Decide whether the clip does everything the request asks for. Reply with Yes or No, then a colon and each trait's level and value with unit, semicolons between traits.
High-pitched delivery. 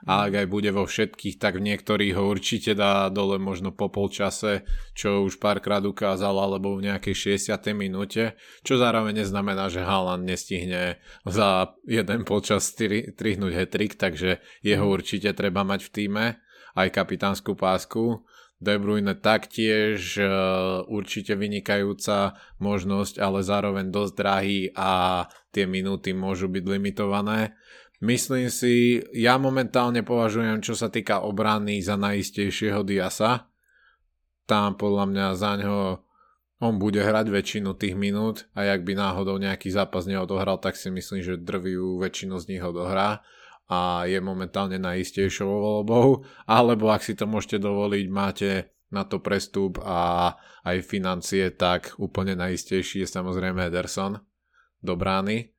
No: low, 100 Hz